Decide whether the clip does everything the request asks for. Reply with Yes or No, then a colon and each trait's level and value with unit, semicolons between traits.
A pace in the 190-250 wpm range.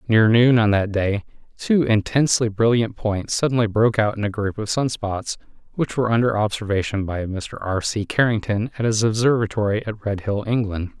No: average, 180 wpm